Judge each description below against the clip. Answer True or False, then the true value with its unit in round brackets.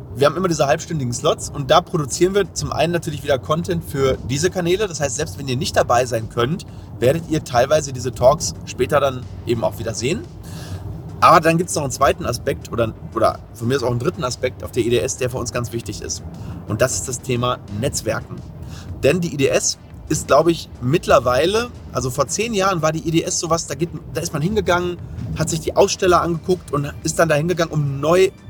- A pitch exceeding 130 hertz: True (140 Hz)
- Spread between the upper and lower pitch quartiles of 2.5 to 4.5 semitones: False (5.6 semitones)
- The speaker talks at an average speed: False (215 wpm)